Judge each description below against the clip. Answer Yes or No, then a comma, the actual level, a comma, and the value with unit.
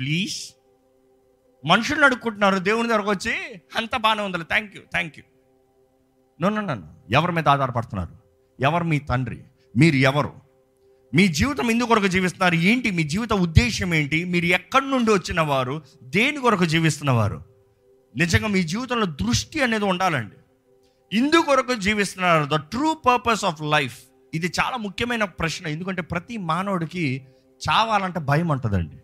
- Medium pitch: Yes, medium, 165 Hz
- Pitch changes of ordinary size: No, wide, 8.0 semitones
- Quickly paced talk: Yes, fast, 130 wpm